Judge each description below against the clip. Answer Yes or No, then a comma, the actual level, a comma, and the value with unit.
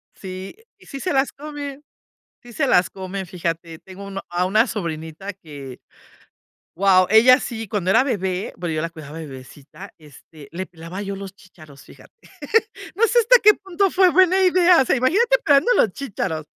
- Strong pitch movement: Yes, wide, 8.8 semitones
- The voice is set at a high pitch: Yes, high, 195 Hz